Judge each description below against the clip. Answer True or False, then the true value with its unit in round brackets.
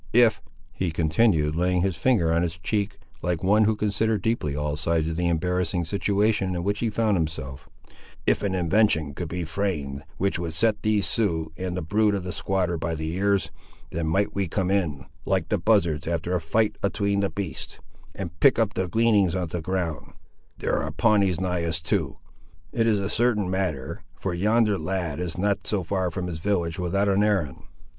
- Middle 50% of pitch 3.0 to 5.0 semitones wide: True (3.7 semitones)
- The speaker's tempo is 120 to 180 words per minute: False (190 wpm)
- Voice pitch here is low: True (90 Hz)